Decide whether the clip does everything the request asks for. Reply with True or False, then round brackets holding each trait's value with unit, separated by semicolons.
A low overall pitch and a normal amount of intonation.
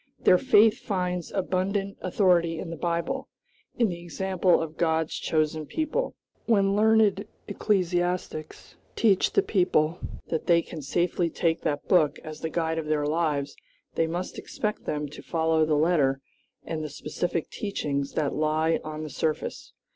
False (170 Hz; 3.2 semitones)